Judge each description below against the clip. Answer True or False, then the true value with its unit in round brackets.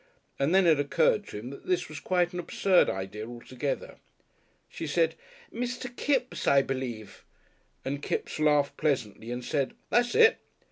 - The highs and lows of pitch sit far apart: True (6.2 semitones)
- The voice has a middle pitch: True (150 Hz)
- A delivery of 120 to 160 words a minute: True (155 wpm)